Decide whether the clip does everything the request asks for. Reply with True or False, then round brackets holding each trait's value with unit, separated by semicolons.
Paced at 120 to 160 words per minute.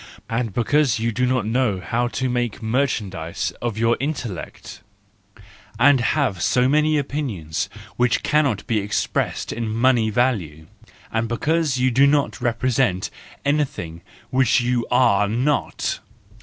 True (135 wpm)